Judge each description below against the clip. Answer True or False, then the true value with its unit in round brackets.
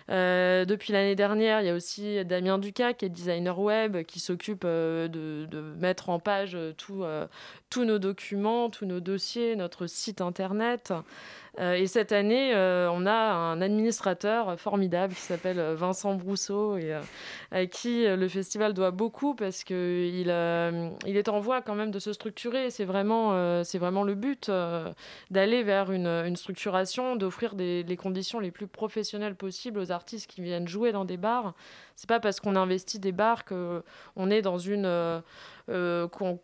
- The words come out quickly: False (180 wpm)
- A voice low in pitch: False (195 Hz)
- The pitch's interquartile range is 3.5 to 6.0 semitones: False (3.0 semitones)